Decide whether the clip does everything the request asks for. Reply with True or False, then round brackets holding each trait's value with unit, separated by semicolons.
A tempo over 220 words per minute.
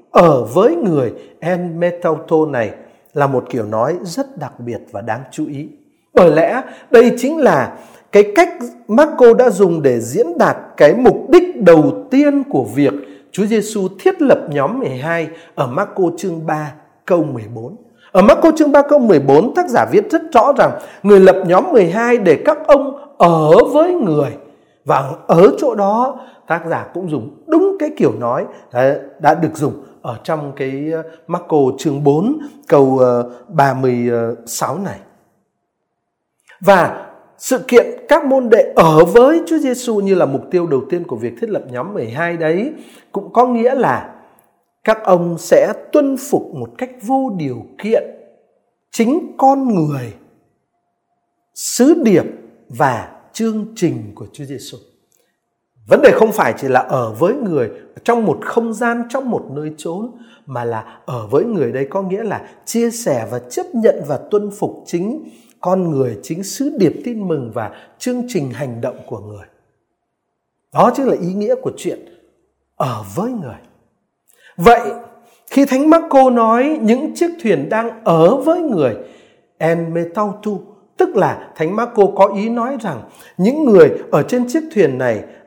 False (165 wpm)